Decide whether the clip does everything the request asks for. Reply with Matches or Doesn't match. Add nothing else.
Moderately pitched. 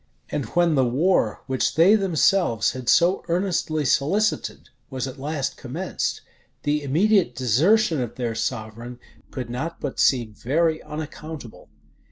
Matches